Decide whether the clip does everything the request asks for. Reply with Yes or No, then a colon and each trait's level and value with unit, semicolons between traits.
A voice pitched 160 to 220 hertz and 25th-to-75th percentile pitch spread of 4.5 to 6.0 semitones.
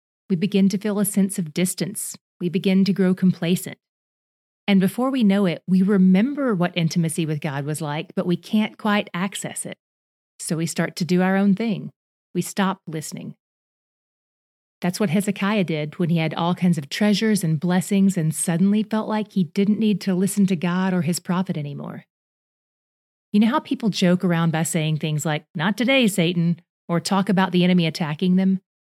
No: medium, 185 Hz; average, 2.9 semitones